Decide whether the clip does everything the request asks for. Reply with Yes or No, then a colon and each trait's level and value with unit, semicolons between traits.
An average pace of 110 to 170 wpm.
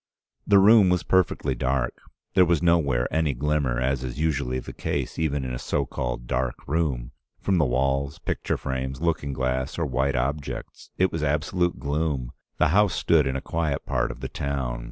No: average, 185 wpm